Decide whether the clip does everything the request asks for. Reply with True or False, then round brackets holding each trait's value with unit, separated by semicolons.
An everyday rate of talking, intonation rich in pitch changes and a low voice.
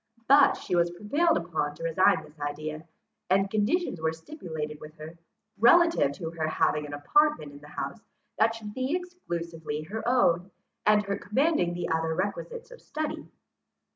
False (165 wpm; 8.3 semitones; 175 Hz)